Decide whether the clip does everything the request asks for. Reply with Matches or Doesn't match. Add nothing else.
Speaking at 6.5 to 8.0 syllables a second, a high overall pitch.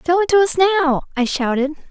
Matches